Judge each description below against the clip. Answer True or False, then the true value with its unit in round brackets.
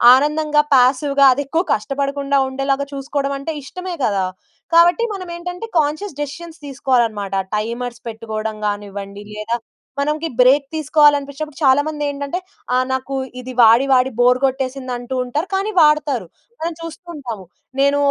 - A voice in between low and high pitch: False (275 Hz)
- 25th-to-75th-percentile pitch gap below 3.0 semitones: False (3.3 semitones)